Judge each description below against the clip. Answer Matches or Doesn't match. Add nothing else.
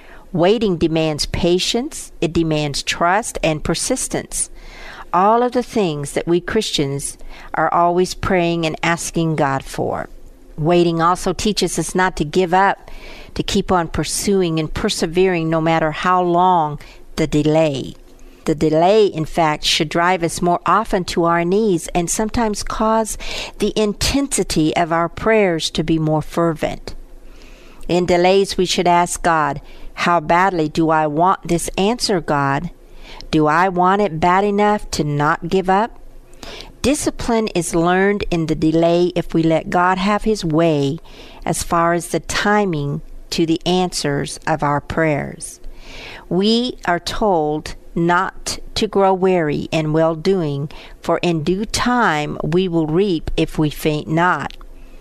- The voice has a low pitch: Doesn't match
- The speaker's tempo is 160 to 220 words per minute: Doesn't match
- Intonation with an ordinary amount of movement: Matches